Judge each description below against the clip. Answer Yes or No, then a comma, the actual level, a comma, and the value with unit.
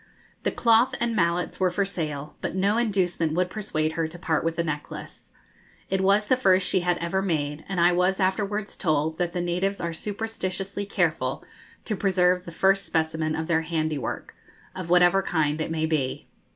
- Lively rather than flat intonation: No, average, 3.3 semitones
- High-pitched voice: No, medium, 180 Hz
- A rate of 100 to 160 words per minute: No, average, 185 wpm